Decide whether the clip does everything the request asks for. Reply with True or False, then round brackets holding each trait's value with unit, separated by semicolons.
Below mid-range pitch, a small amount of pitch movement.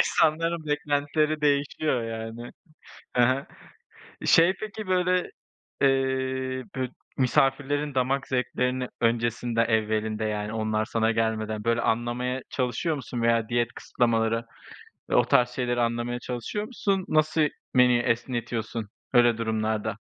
False (125 Hz; 3.5 semitones)